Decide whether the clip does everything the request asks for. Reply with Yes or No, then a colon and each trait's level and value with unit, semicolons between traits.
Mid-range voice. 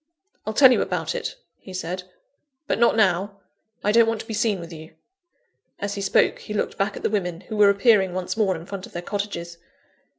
No: high, 200 Hz